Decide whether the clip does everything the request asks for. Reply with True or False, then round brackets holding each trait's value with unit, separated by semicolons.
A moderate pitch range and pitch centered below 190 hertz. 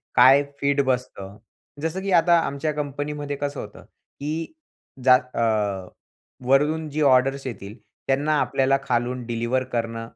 True (3.6 semitones; 135 Hz)